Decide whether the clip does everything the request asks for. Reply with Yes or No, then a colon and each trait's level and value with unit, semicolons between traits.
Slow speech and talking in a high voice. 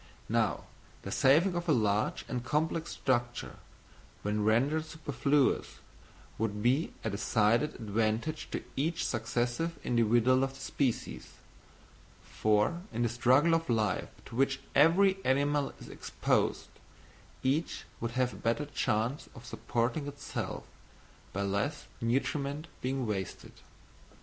No: slow, 125 wpm; low, 130 Hz